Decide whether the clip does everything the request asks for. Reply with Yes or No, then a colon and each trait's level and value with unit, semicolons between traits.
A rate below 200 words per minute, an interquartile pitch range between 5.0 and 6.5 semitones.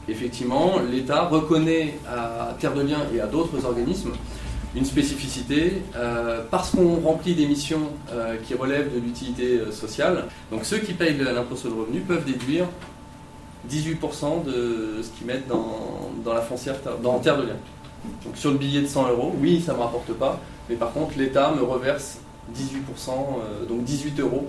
No: average, 175 wpm; average, 4.0 semitones